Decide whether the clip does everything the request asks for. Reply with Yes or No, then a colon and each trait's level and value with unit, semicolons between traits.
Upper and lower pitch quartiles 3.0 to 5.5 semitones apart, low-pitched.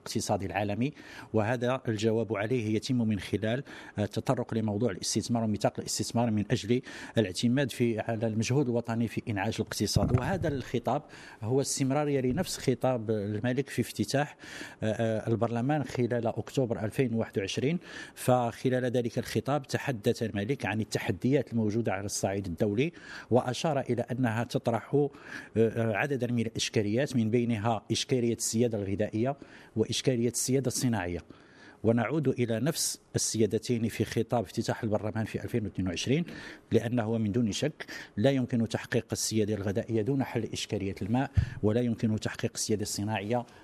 No: narrow, 2.5 semitones; low, 115 Hz